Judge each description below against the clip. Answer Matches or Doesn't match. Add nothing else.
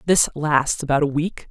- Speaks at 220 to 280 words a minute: Doesn't match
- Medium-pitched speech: Matches